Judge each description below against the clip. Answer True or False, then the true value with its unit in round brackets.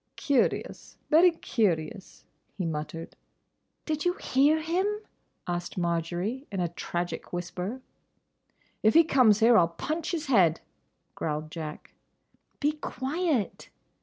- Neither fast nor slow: False (120 wpm)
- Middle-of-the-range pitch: False (215 Hz)